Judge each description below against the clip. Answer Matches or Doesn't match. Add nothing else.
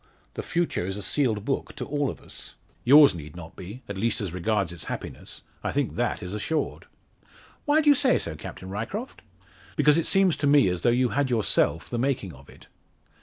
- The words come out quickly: Matches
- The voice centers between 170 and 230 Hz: Doesn't match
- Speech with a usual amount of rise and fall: Doesn't match